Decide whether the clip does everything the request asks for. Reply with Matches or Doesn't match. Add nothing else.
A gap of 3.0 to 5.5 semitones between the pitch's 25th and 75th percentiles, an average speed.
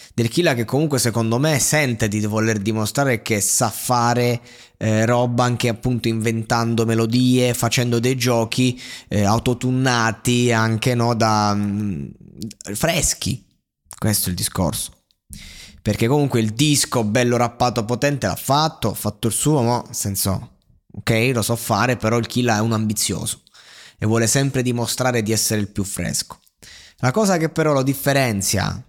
Doesn't match